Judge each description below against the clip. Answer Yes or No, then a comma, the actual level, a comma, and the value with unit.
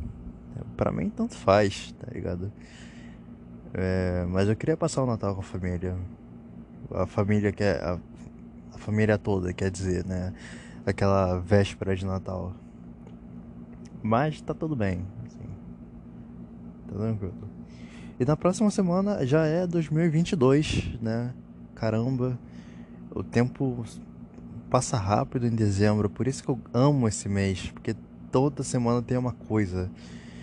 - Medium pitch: No, low, 100 Hz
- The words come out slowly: No, average, 130 wpm